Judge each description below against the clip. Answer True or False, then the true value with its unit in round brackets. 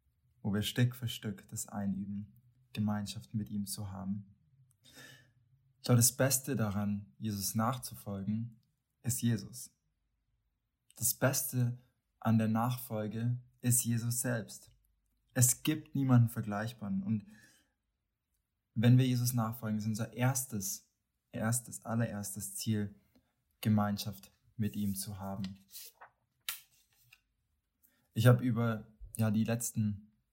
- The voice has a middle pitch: False (110 Hz)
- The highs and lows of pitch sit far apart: False (2.9 semitones)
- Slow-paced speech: True (105 wpm)